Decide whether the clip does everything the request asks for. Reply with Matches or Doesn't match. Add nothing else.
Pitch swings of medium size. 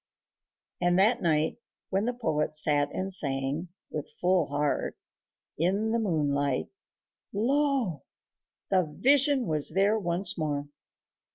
Doesn't match